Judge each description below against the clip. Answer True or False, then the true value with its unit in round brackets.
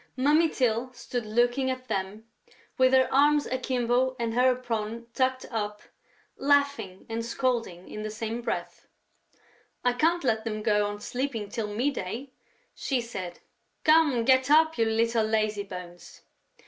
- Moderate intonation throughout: True (3.3 semitones)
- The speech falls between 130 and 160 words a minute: True (145 wpm)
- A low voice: False (235 Hz)